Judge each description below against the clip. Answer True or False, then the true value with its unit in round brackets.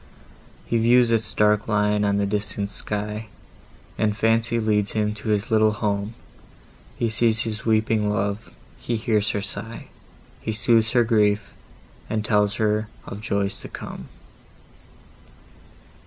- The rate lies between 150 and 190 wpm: False (135 wpm)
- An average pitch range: False (1.3 semitones)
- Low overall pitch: True (105 Hz)